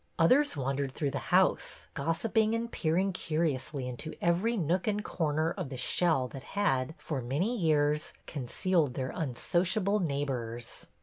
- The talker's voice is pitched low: No, medium, 160 Hz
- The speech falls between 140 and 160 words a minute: Yes, average, 150 wpm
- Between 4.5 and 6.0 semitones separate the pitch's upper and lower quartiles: Yes, wide, 5.4 semitones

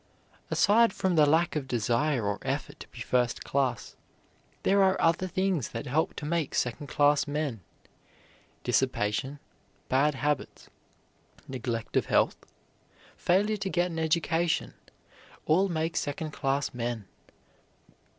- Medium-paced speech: No, slow, 130 wpm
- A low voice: No, medium, 150 Hz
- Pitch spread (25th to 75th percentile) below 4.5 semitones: No, average, 5.0 semitones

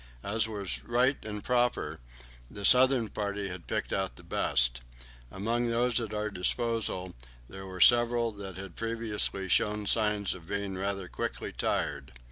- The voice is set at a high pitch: No, low, 105 Hz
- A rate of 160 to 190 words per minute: No, average, 150 wpm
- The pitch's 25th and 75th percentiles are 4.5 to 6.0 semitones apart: No, average, 3.3 semitones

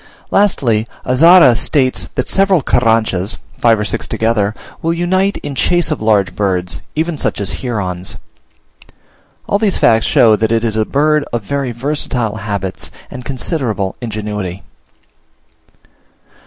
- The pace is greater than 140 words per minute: No, slow, 135 wpm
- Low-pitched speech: Yes, low, 115 Hz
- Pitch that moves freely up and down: Yes, wide, 6.0 semitones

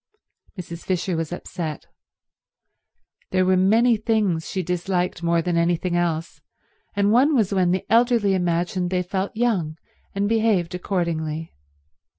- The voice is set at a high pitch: No, medium, 180 Hz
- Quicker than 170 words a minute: No, slow, 135 wpm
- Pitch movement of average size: Yes, average, 3.1 semitones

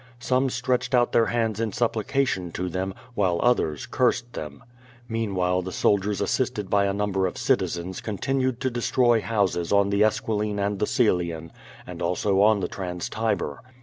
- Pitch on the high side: No, low, 105 Hz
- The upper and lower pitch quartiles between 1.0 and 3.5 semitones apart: No, average, 4.4 semitones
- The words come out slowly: No, average, 165 wpm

